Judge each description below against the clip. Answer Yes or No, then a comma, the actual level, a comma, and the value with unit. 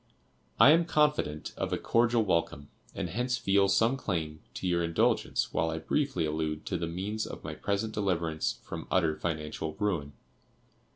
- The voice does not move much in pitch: No, wide, 5.5 semitones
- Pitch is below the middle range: Yes, very low, 90 Hz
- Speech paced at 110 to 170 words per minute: Yes, average, 165 wpm